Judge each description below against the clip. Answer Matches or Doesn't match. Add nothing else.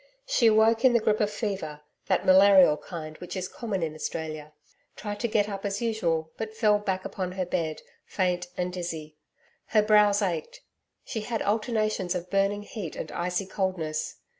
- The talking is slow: Doesn't match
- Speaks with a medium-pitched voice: Doesn't match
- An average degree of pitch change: Matches